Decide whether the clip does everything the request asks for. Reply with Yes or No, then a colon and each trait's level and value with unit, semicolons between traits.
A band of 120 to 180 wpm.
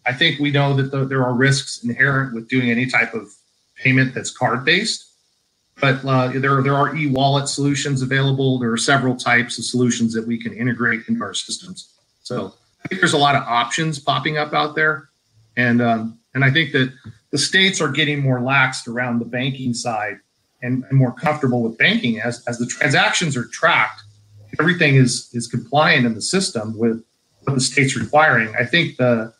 No: average, 190 wpm